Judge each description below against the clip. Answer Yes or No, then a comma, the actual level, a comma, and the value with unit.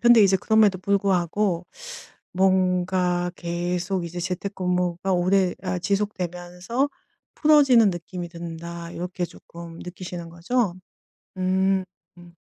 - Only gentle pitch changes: Yes, narrow, 1.9 semitones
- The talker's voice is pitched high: No, medium, 180 Hz